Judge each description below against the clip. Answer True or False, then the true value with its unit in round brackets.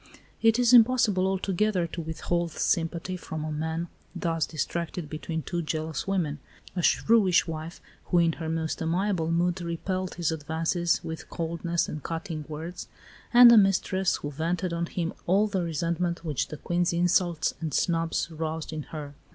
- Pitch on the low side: False (170 Hz)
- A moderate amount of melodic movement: False (2.2 semitones)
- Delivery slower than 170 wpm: True (160 wpm)